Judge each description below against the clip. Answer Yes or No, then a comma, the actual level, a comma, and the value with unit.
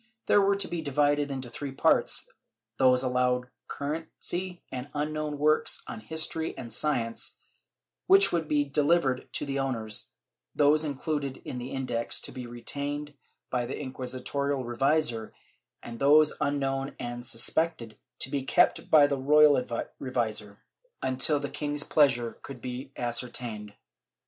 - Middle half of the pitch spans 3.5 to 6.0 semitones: No, average, 3.1 semitones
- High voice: No, low, 135 Hz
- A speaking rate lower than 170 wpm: Yes, average, 140 wpm